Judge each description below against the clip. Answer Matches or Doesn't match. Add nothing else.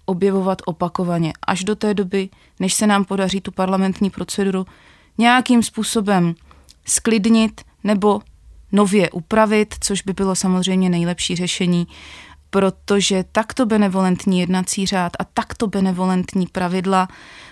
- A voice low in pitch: Doesn't match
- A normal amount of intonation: Doesn't match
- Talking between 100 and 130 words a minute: Matches